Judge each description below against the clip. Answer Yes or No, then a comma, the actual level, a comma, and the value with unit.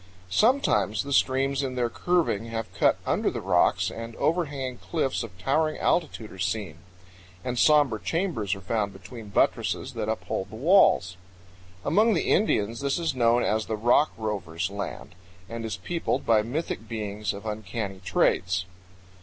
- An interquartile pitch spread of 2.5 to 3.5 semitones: No, wide, 5.6 semitones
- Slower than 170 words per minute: Yes, average, 155 wpm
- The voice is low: Yes, low, 115 Hz